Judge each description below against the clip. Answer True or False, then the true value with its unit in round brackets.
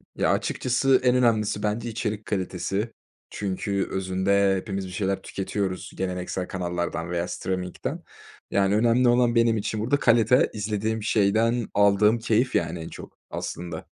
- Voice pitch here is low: True (105 Hz)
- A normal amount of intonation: True (3.5 semitones)